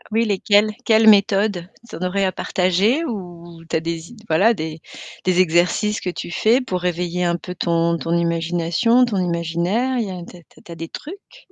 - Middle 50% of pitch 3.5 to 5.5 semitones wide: Yes, average, 4.1 semitones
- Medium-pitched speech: Yes, medium, 180 Hz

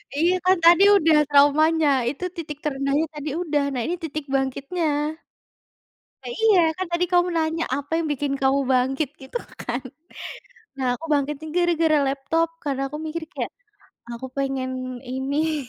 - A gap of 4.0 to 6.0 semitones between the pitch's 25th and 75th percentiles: No, average, 3.3 semitones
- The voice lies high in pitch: Yes, very high, 295 Hz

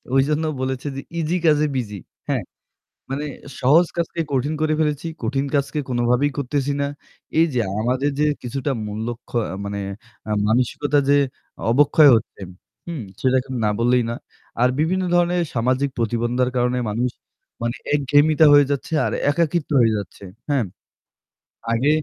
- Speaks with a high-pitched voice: No, low, 135 Hz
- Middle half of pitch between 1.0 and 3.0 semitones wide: No, average, 3.5 semitones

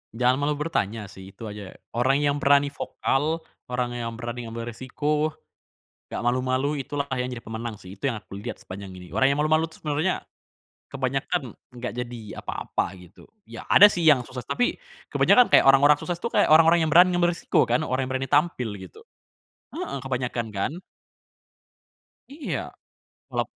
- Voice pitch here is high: No, low, 130 Hz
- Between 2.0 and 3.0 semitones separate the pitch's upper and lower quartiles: No, average, 4.2 semitones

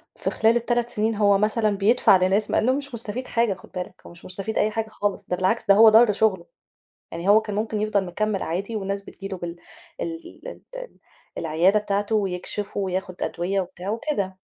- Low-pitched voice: No, high, 205 Hz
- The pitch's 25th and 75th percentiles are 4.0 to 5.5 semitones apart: No, average, 2.7 semitones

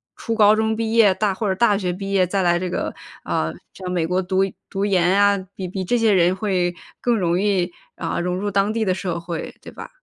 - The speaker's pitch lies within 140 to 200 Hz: Yes, high, 190 Hz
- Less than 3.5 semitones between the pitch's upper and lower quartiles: Yes, narrow, 2.4 semitones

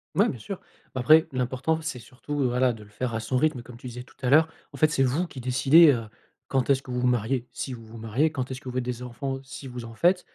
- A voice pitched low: Yes, low, 130 Hz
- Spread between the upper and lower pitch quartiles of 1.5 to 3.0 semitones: Yes, narrow, 2.5 semitones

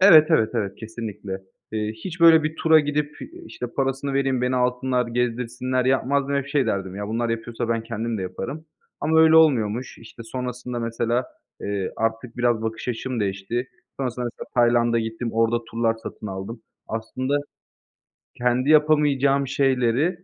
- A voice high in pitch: No, low, 125 Hz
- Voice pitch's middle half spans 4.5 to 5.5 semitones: No, average, 3.3 semitones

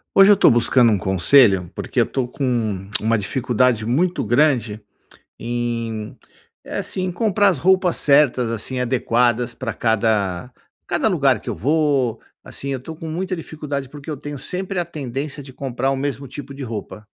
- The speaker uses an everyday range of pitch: Yes, average, 4.5 semitones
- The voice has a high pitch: No, low, 130 Hz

